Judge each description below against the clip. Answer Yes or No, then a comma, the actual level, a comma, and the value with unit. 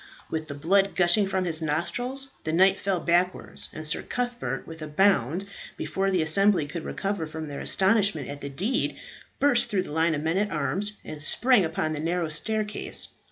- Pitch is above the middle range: No, medium, 175 Hz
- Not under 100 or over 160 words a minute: No, average, 190 wpm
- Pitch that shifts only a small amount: No, average, 4.3 semitones